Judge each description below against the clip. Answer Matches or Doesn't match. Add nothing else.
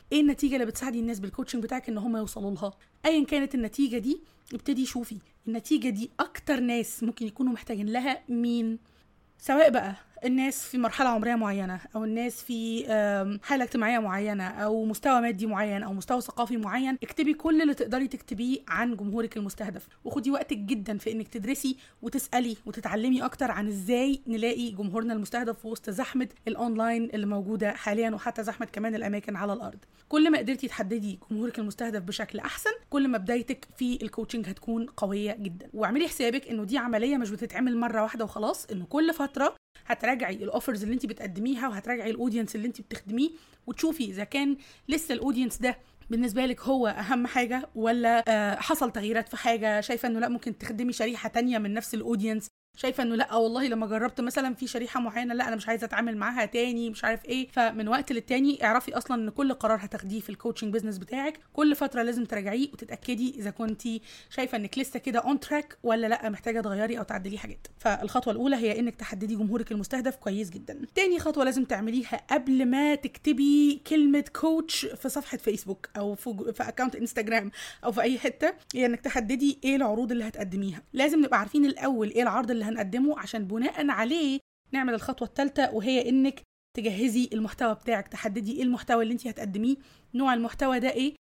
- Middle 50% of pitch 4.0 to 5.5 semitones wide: Doesn't match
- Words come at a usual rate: Doesn't match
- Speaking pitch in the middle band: Doesn't match